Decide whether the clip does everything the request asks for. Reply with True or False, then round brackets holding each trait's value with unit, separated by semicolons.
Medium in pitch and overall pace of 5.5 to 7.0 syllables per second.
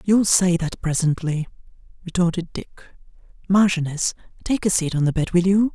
False (175 Hz; 5.0 syllables/s)